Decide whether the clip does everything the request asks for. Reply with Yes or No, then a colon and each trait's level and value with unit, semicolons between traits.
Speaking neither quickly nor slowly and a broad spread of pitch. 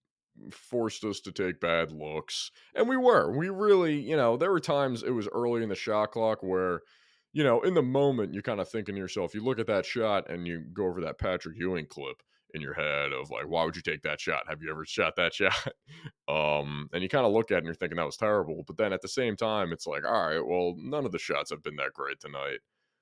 No: fast, 260 wpm; wide, 8.4 semitones